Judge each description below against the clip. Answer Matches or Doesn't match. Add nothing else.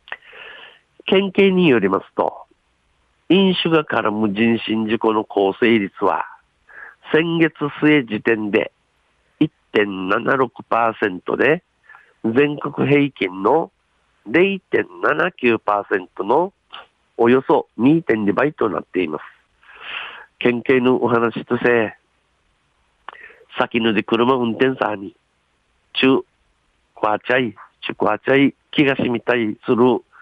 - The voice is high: Doesn't match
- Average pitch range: Matches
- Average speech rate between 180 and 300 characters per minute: Doesn't match